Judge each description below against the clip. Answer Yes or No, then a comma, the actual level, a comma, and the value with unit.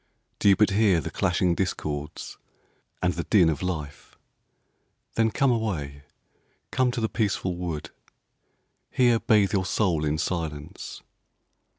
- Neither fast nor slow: No, slow, 130 wpm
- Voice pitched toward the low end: Yes, very low, 90 Hz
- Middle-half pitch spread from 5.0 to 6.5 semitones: Yes, wide, 5.6 semitones